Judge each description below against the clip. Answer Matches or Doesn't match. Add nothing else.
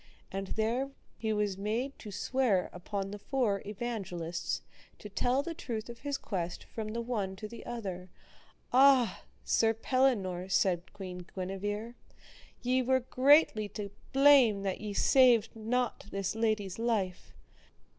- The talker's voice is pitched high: Matches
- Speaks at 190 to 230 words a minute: Doesn't match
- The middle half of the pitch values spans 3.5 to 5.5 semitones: Matches